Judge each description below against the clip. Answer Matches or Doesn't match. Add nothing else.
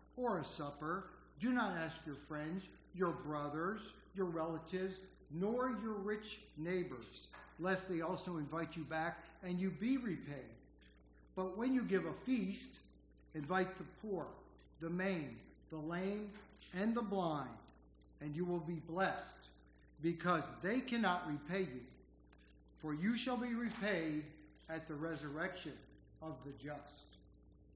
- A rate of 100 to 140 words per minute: Matches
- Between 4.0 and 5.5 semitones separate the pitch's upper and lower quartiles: Matches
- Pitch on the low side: Doesn't match